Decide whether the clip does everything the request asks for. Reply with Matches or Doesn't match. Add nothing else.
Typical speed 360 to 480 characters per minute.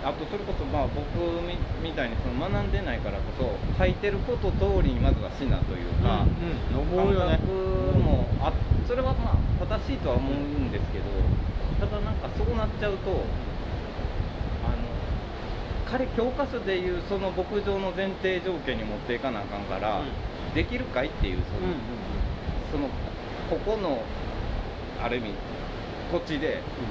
Doesn't match